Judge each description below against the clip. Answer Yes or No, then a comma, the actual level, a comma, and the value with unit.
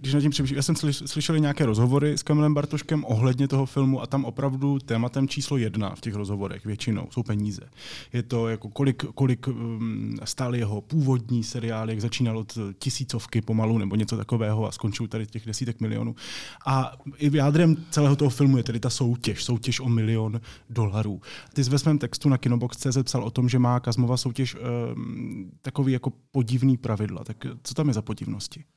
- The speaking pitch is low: Yes, low, 125 Hz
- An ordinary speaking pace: No, fast, 185 wpm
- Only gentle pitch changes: No, average, 3.5 semitones